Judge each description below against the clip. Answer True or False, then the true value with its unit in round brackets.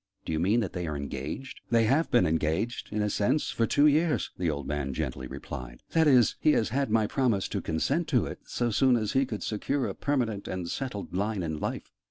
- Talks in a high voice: False (110 Hz)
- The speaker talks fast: True (230 wpm)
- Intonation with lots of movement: True (7.9 semitones)